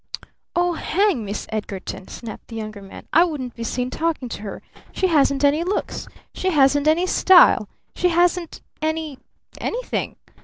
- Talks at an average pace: Yes, average, 155 wpm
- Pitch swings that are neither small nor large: No, wide, 6.6 semitones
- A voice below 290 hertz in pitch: No, very high, 300 Hz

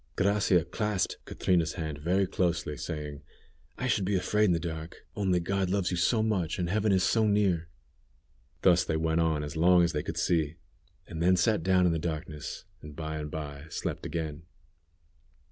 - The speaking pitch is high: No, very low, 85 Hz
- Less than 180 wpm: No, average, 185 wpm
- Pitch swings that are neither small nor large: Yes, average, 3.1 semitones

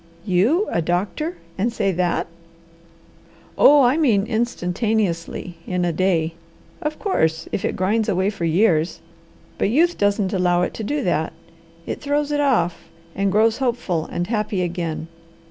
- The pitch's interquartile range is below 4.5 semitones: No, average, 5.3 semitones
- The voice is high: Yes, high, 200 Hz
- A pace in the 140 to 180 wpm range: Yes, average, 150 wpm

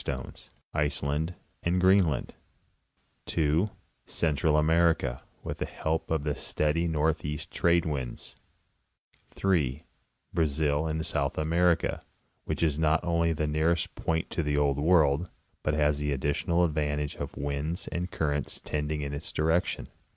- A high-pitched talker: No, very low, 75 Hz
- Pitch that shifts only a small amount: Yes, narrow, 2.3 semitones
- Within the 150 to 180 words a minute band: No, slow, 135 wpm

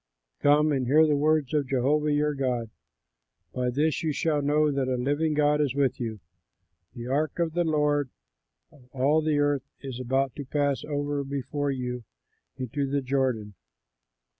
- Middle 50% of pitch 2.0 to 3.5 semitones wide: Yes, narrow, 2.5 semitones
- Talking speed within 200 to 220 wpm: No, average, 165 wpm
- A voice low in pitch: No, medium, 145 Hz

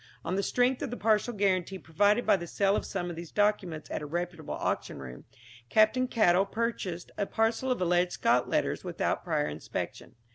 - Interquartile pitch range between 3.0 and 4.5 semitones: Yes, average, 4.1 semitones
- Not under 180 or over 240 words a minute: Yes, average, 190 wpm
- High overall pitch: Yes, high, 195 Hz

